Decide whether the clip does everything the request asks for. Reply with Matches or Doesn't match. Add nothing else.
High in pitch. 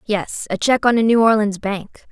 Matches